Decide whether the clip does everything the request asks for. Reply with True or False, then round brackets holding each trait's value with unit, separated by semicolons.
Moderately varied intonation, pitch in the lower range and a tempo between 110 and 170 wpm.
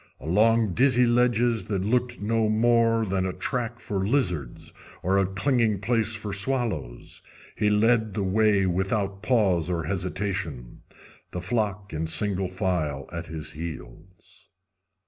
True (3.9 semitones; 100 Hz; 135 wpm)